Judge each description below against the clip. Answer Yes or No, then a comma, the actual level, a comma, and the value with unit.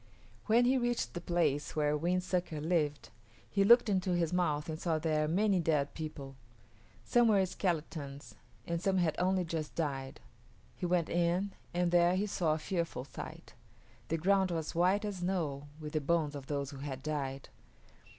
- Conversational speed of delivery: Yes, average, 175 wpm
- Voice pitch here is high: No, medium, 170 Hz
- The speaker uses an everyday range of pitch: Yes, average, 3.6 semitones